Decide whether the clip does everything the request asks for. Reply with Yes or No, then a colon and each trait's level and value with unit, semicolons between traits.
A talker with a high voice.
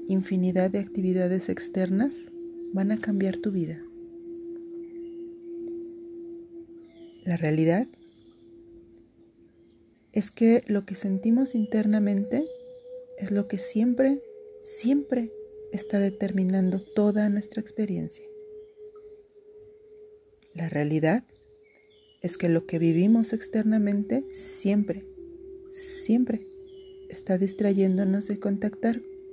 Yes: high, 230 Hz